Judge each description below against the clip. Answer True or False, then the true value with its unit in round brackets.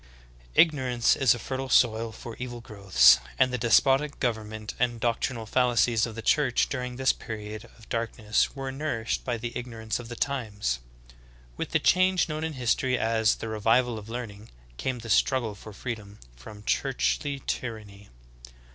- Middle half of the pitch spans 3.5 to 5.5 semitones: False (2.8 semitones)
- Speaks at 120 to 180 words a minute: True (165 wpm)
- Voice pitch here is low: True (115 Hz)